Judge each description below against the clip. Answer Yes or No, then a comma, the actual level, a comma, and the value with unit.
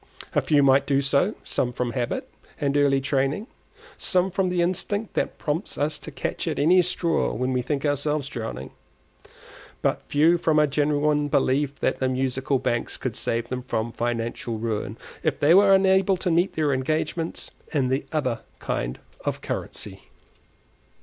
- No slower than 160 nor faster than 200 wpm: Yes, average, 165 wpm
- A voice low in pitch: No, medium, 145 Hz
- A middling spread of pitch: Yes, average, 4.3 semitones